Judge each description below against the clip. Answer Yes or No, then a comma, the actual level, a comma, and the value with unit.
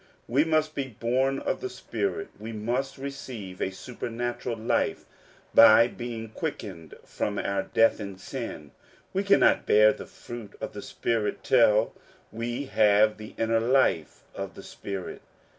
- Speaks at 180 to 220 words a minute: No, average, 145 wpm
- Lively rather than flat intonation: No, average, 3.8 semitones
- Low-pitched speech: Yes, low, 115 Hz